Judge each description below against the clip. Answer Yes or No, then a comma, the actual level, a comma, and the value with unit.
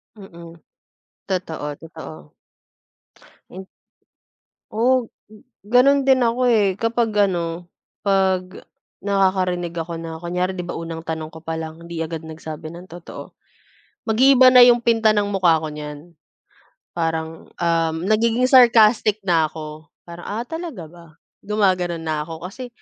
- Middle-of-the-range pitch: Yes, medium, 180 Hz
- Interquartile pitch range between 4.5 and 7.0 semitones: Yes, average, 5.0 semitones